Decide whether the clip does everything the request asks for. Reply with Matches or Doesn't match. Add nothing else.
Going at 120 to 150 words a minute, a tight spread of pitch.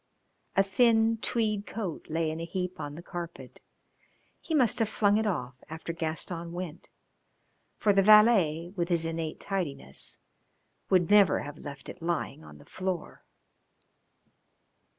Doesn't match